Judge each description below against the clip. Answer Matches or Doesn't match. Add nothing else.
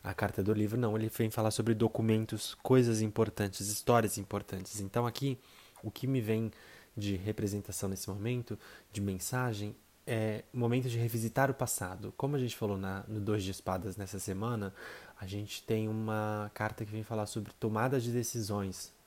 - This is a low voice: Matches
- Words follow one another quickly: Doesn't match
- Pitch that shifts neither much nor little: Doesn't match